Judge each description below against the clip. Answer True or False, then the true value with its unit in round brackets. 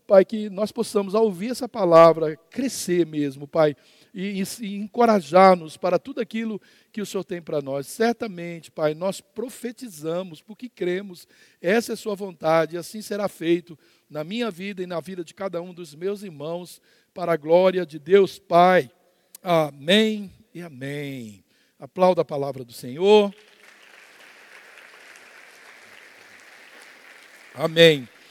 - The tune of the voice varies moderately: True (4.2 semitones)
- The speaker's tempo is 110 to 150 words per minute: True (140 wpm)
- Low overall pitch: False (180 Hz)